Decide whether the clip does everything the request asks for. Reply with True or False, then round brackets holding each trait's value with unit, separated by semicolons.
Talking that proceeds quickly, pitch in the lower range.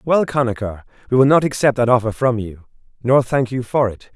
True (215 wpm; 125 Hz)